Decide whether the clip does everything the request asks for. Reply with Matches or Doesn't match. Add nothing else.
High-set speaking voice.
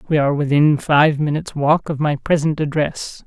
Doesn't match